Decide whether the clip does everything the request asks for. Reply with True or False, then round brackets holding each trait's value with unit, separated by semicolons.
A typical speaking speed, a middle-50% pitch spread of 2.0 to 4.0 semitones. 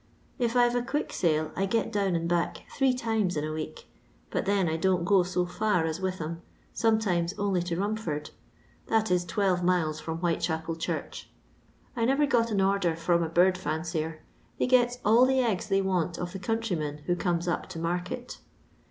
False (190 wpm; 4.5 semitones)